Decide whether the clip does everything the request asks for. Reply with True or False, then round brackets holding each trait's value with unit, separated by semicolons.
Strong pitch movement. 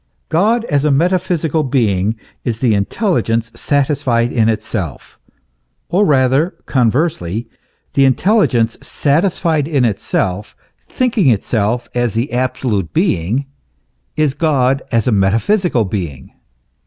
True (5.8 semitones)